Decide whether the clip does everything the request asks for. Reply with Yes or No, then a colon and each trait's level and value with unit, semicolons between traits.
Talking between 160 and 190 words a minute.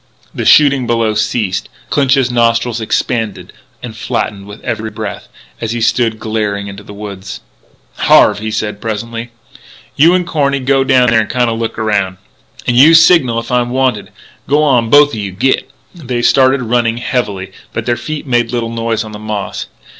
Yes: average, 170 wpm